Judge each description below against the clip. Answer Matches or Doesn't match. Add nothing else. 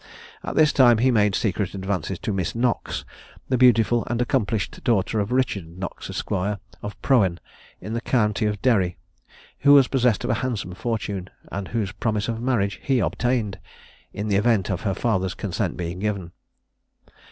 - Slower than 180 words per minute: Matches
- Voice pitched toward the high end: Doesn't match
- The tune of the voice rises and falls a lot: Doesn't match